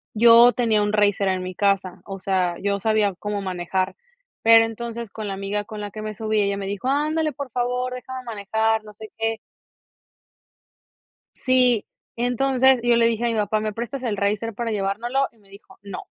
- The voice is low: No, high, 215 Hz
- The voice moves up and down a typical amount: Yes, average, 3.0 semitones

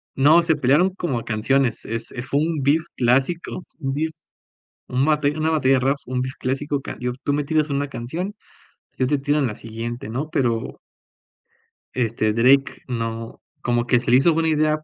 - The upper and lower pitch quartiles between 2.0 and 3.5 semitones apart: No, average, 3.9 semitones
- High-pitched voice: No, low, 135 Hz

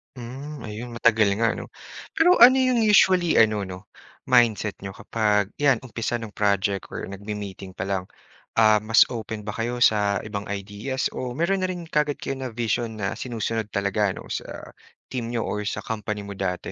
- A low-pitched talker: Yes, low, 110 Hz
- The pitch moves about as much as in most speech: Yes, average, 3.8 semitones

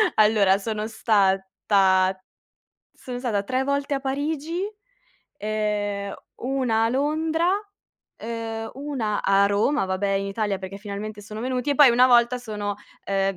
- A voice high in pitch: Yes, high, 220 Hz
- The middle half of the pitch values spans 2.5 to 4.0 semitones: No, average, 4.5 semitones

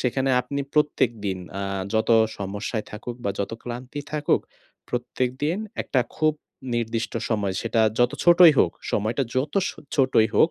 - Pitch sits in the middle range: No, low, 120 Hz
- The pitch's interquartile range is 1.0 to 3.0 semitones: No, average, 4.3 semitones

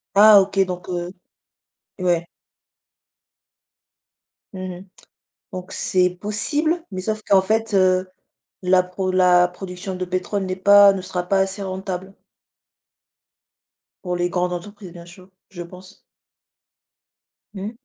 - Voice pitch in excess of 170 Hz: Yes, medium, 185 Hz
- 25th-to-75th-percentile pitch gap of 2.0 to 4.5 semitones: No, narrow, 1.6 semitones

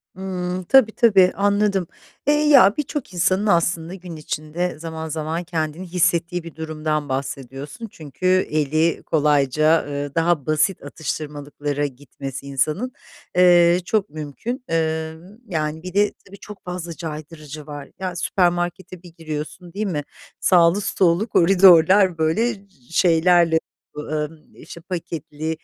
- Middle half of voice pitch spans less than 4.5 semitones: Yes, average, 3.2 semitones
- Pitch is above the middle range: No, medium, 165 Hz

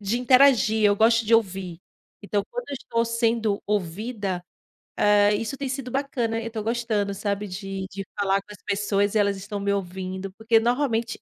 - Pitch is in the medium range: No, high, 210 Hz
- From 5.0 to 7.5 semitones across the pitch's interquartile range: No, average, 2.7 semitones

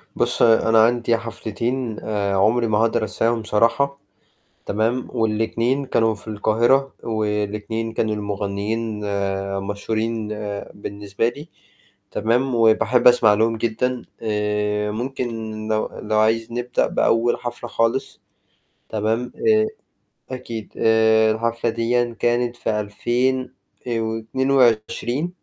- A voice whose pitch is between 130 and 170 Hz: No, low, 115 Hz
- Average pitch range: No, narrow, 2.0 semitones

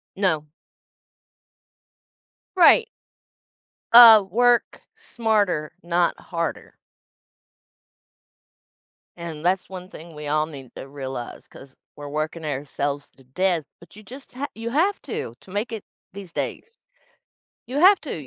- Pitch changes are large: Yes, wide, 7.5 semitones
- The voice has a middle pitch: Yes, medium, 180 Hz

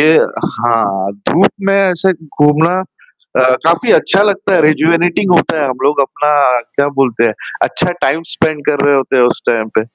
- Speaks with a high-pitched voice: No, medium, 150 Hz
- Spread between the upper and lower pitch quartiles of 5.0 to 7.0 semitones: Yes, average, 5.3 semitones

